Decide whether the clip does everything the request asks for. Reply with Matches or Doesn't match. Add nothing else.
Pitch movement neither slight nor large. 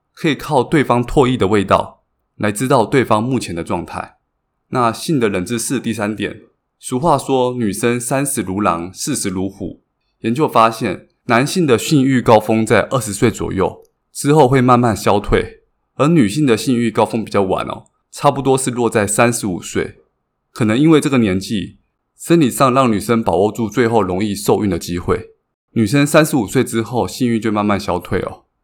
Matches